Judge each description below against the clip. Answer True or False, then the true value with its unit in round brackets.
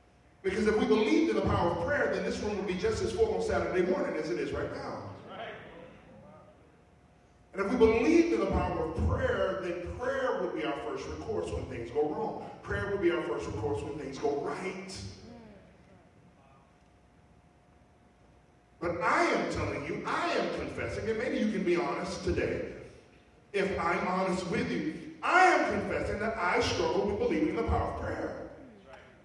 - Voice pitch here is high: True (230 Hz)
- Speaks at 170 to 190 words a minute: True (180 wpm)